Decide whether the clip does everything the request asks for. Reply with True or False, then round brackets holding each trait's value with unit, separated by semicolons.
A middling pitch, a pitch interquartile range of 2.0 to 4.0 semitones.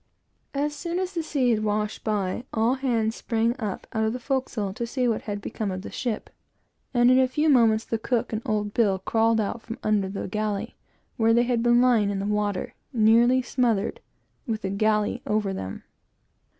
False (225 Hz; 2.8 semitones)